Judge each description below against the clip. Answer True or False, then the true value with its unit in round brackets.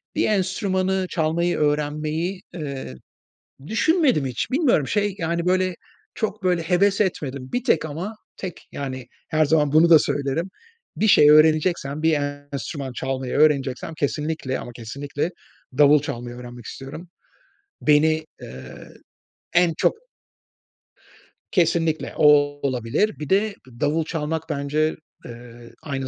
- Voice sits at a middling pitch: True (155 Hz)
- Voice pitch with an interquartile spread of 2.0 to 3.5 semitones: False (4.3 semitones)